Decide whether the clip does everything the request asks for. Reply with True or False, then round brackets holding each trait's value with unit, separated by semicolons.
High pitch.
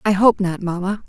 True (195 Hz)